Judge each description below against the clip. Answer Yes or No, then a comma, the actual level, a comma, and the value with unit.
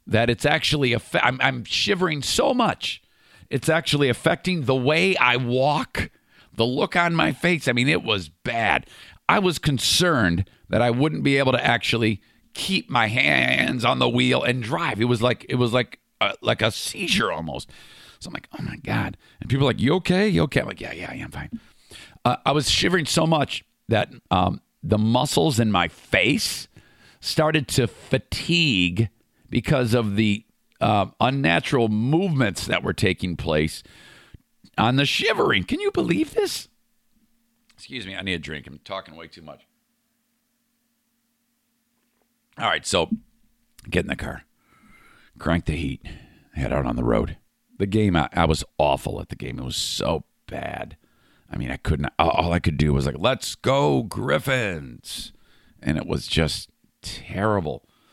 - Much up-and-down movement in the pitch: Yes, wide, 8.5 semitones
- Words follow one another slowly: No, average, 175 wpm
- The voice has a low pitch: Yes, low, 125 Hz